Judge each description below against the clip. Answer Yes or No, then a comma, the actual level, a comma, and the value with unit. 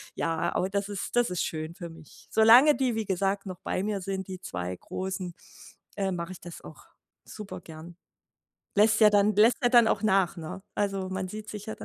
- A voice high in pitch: Yes, high, 195 Hz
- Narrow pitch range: No, average, 3.1 semitones